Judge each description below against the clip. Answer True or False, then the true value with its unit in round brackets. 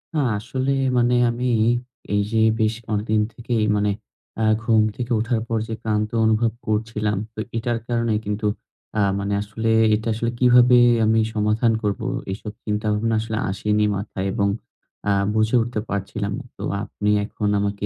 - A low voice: True (110 Hz)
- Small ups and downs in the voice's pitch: True (1.9 semitones)